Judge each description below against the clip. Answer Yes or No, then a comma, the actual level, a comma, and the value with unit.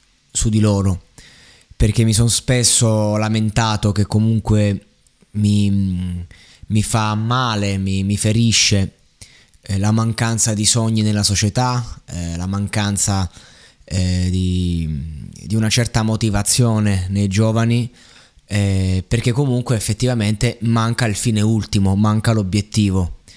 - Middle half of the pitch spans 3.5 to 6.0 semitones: No, narrow, 2.5 semitones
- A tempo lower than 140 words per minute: Yes, slow, 115 wpm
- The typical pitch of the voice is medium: No, low, 105 Hz